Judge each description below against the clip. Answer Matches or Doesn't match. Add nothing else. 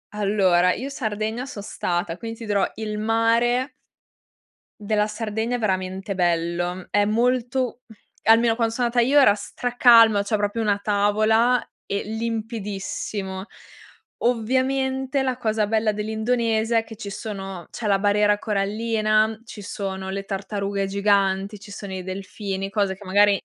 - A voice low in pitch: Doesn't match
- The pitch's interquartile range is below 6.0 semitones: Matches